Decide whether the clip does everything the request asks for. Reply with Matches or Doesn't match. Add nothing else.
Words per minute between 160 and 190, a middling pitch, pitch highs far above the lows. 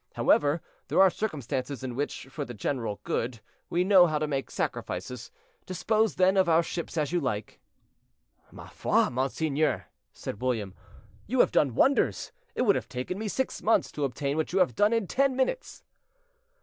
Matches